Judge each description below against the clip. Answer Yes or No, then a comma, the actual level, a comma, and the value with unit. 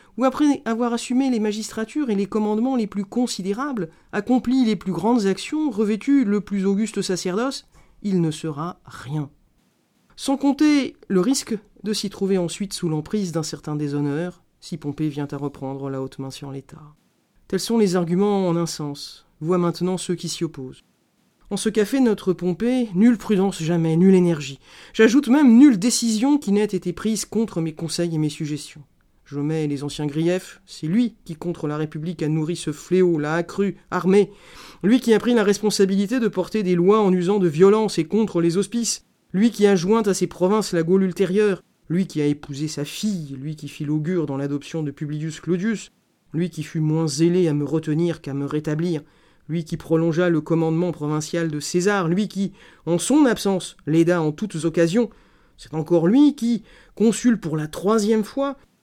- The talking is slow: No, average, 190 wpm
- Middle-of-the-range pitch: Yes, medium, 180 Hz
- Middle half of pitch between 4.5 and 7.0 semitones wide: Yes, average, 5.2 semitones